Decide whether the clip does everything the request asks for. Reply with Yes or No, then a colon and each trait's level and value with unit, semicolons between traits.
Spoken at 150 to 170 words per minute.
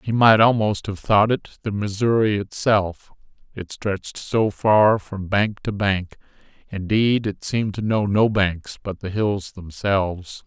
Yes: average, 160 wpm